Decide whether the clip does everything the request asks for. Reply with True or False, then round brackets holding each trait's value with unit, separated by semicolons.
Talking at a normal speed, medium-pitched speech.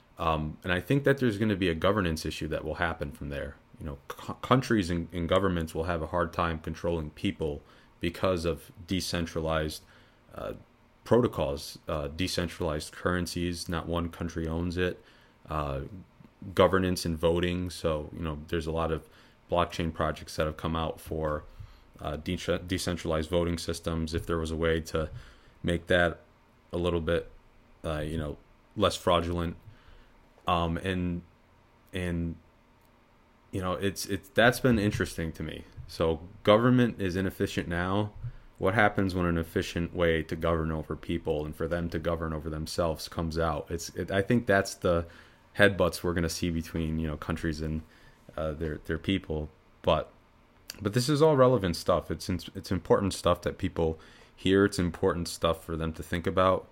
False (170 wpm; 85 Hz)